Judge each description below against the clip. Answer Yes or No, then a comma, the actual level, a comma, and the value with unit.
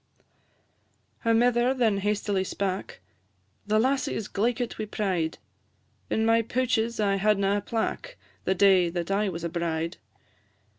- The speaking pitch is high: Yes, high, 210 Hz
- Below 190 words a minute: Yes, average, 140 wpm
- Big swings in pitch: No, average, 3.3 semitones